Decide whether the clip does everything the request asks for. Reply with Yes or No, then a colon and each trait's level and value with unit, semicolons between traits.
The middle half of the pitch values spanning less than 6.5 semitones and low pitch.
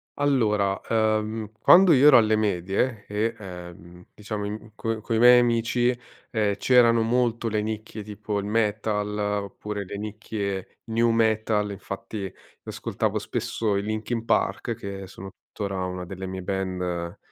Yes: narrow, 2.4 semitones; low, 105 Hz